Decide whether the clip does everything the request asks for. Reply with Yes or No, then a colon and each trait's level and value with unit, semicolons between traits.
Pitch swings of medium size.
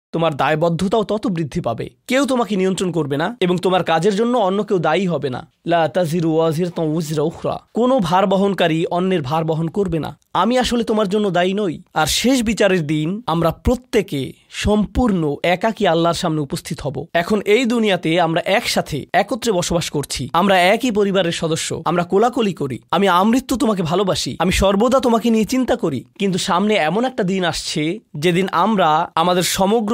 Yes: average, 4.6 semitones